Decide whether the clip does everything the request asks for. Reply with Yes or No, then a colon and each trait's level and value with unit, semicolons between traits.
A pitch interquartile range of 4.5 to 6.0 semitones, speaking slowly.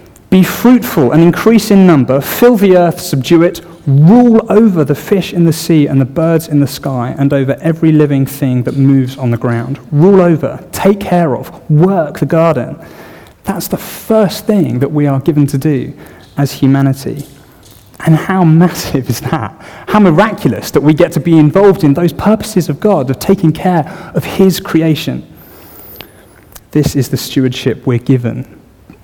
No: average, 4.8 semitones; average, 175 wpm